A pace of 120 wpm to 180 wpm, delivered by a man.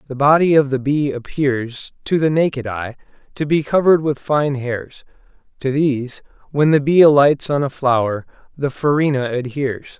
Yes: average, 170 wpm; male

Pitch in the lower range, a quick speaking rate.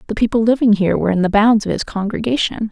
No: high, 215 Hz; fast, 245 wpm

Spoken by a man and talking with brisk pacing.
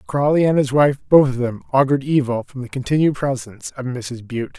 Yes: male; fast, 210 wpm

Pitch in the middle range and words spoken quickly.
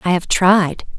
No: medium, 180 Hz; average, 185 wpm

